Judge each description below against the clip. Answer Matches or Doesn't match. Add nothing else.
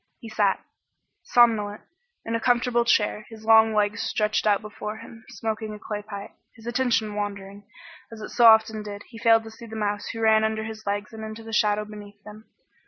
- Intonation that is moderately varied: Doesn't match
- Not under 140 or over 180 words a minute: Doesn't match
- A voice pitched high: Matches